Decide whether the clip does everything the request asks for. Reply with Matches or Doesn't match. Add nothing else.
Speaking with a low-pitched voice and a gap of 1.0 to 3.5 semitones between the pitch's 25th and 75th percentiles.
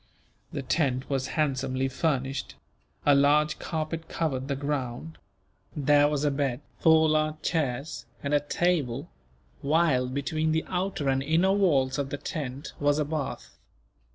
Doesn't match